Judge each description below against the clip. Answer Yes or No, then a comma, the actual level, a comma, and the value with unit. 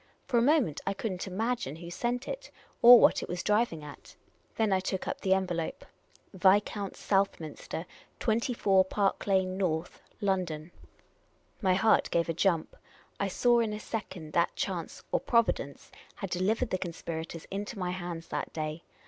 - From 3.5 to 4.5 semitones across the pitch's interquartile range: Yes, average, 3.9 semitones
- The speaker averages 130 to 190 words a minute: Yes, average, 165 wpm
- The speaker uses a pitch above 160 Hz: Yes, high, 190 Hz